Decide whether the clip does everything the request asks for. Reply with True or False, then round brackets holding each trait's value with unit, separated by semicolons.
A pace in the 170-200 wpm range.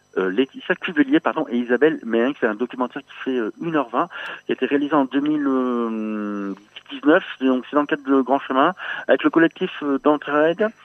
True (190 wpm)